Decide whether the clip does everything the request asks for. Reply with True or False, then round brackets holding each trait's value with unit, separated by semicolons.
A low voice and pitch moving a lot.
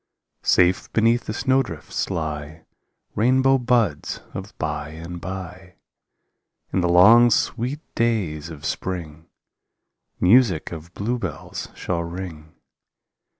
True (90 Hz; 6.4 semitones)